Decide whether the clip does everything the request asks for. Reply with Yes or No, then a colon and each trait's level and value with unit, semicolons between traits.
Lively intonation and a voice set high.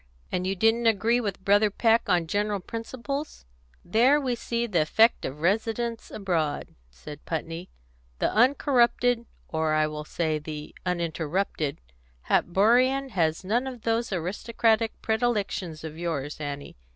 Yes: wide, 6.4 semitones; high, 200 Hz